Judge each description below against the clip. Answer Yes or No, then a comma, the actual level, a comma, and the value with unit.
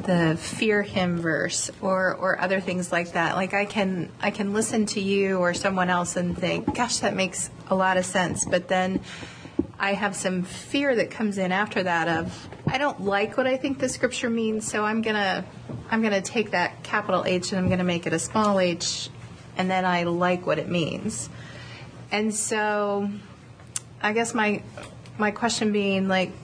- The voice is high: Yes, high, 195 Hz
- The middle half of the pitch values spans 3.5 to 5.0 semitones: No, average, 2.8 semitones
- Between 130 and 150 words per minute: No, average, 195 wpm